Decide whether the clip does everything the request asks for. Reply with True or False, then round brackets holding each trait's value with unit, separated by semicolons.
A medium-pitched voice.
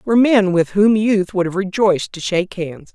False (195 Hz)